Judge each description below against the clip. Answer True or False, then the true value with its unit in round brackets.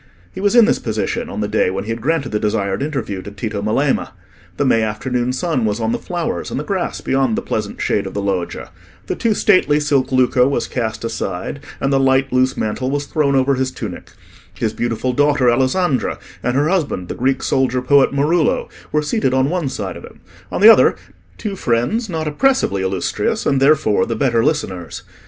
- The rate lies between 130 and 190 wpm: False (205 wpm)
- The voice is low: True (130 Hz)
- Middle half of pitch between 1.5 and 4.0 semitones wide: False (5.0 semitones)